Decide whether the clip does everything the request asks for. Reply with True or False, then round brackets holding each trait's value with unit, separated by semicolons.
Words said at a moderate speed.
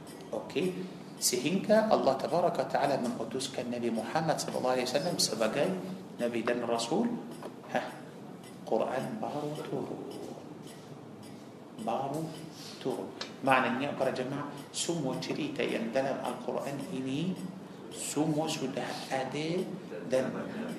True (105 wpm)